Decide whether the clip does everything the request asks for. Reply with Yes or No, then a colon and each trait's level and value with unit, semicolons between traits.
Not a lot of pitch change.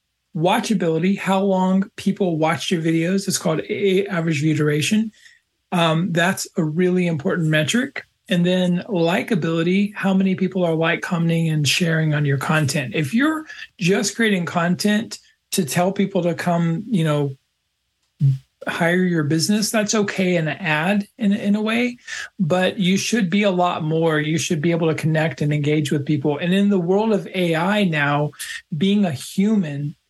No: average, 3.8 semitones